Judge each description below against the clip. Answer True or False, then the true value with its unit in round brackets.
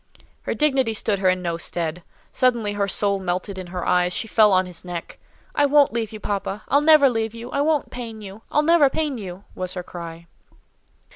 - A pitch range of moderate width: False (5.8 semitones)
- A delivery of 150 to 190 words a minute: False (205 wpm)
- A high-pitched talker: True (205 Hz)